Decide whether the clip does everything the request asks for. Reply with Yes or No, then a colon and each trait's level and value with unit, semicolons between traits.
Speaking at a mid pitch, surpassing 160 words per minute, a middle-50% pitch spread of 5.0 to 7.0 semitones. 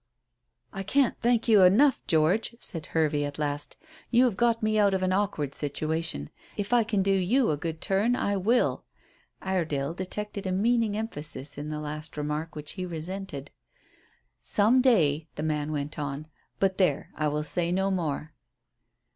Yes: medium, 180 Hz; average, 170 wpm; wide, 5.4 semitones